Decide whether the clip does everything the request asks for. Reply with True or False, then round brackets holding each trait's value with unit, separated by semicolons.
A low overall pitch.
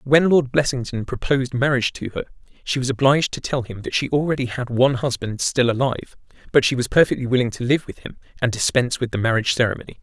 True (125 Hz)